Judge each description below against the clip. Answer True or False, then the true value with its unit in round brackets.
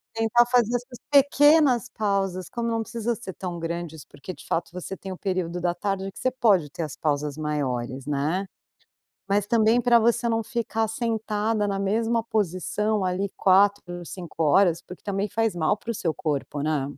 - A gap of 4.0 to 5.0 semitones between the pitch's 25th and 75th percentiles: True (4.7 semitones)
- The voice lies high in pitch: True (200 Hz)